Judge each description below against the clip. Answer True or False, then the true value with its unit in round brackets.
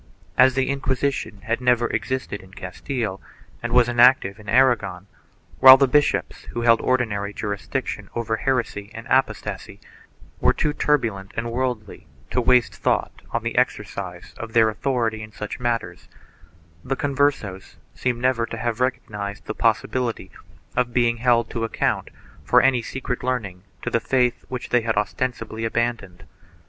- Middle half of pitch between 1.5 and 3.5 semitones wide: True (3.0 semitones)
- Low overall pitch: True (120 Hz)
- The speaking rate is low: False (155 wpm)